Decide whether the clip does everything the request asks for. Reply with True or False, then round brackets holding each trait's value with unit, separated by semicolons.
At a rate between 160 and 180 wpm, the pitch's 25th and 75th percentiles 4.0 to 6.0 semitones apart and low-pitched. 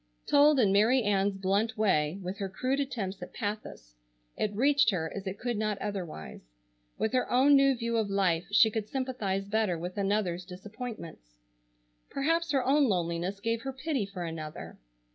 False (170 wpm; 5.0 semitones; 205 Hz)